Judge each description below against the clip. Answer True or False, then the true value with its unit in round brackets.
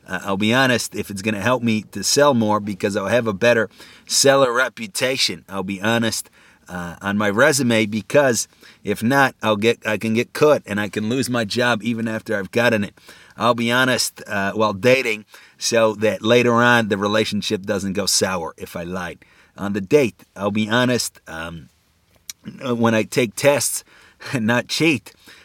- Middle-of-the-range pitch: False (110 Hz)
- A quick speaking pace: False (185 wpm)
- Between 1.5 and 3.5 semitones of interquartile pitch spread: True (2.9 semitones)